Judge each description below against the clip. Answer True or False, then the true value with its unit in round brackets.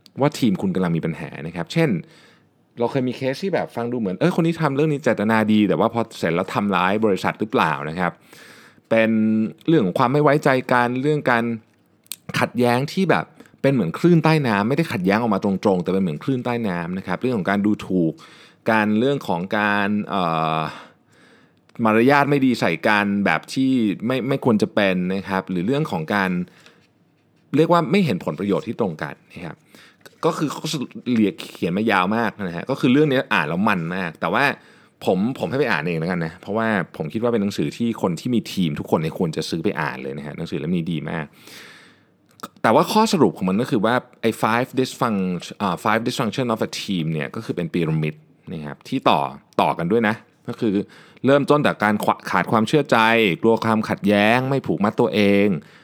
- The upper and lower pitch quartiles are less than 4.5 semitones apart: False (5.6 semitones)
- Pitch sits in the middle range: False (115 Hz)